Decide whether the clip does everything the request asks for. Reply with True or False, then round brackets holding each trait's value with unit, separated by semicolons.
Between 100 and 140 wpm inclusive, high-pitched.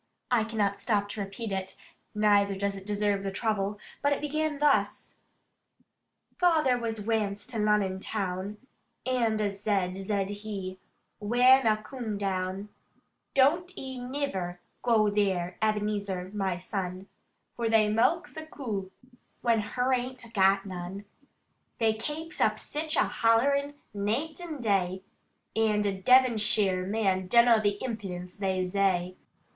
True (135 wpm; 210 Hz)